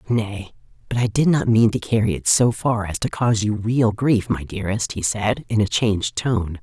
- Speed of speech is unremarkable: No, fast, 225 wpm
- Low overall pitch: Yes, low, 110 Hz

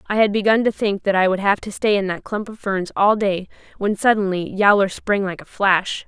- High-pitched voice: Yes, high, 200 Hz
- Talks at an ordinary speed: No, fast, 245 wpm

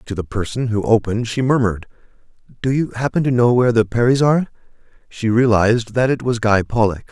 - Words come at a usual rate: Yes, average, 195 wpm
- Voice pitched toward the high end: No, low, 115 Hz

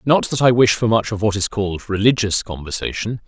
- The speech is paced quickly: Yes, fast, 220 wpm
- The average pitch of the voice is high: No, low, 110 Hz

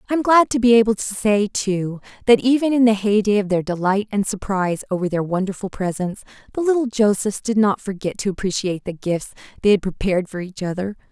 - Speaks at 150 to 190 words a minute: No, fast, 205 wpm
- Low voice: No, high, 205 Hz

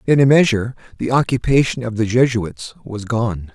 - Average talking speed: Yes, average, 170 wpm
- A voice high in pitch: No, low, 120 Hz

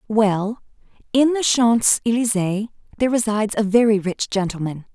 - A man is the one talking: No, female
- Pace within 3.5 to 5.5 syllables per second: Yes, 5.0 syllables/s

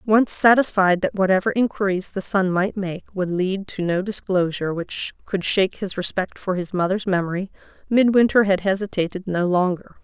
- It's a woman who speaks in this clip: Yes, female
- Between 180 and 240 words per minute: No, average, 165 wpm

